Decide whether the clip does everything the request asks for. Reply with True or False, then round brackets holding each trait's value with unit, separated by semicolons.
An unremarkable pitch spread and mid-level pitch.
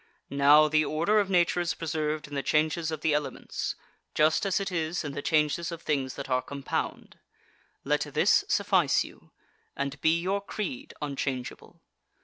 True (3.2 semitones; 155 Hz)